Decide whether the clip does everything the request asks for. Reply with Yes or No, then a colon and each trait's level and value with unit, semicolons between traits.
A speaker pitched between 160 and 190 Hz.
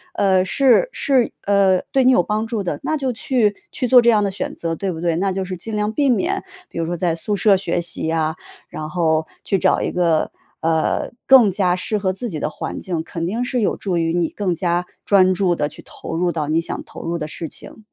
Yes: medium, 185 Hz